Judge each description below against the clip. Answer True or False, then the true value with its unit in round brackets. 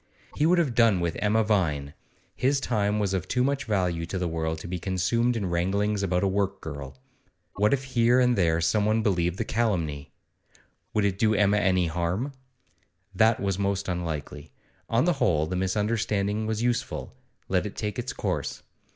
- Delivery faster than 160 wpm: True (180 wpm)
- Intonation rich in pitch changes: False (4.1 semitones)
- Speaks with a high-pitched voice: False (100 Hz)